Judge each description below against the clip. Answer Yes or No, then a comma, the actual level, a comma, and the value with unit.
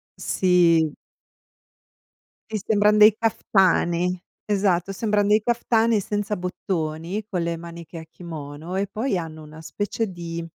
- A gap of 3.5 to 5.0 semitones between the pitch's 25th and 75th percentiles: Yes, average, 3.8 semitones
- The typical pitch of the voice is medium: Yes, medium, 180 Hz